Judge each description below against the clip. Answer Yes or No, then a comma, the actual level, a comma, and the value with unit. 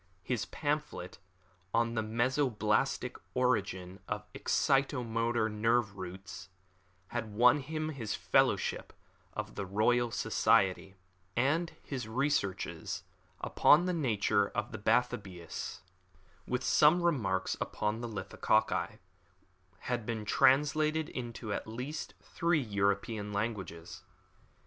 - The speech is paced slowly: Yes, slow, 100 wpm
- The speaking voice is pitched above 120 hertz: No, low, 115 Hz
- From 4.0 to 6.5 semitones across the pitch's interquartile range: Yes, average, 4.7 semitones